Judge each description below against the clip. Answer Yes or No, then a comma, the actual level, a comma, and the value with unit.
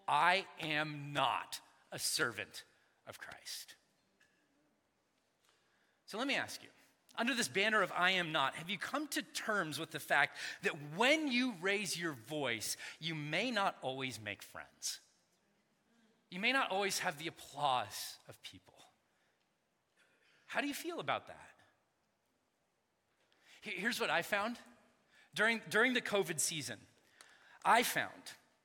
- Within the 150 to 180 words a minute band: No, slow, 135 wpm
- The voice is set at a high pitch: Yes, high, 195 Hz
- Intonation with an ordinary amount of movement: No, wide, 6.9 semitones